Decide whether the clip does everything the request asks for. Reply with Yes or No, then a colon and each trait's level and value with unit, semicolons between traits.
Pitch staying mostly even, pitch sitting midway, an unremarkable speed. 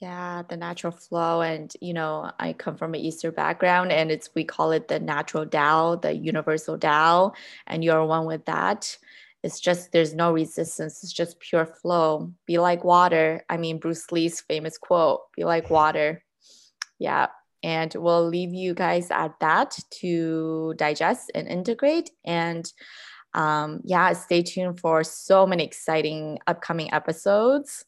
Yes: narrow, 1.8 semitones; medium, 165 Hz; average, 155 wpm